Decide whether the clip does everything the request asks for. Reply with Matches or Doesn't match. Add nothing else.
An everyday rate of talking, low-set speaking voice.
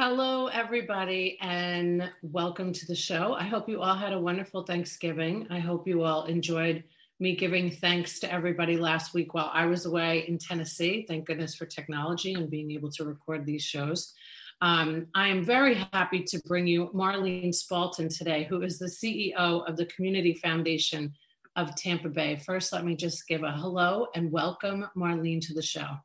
Doesn't match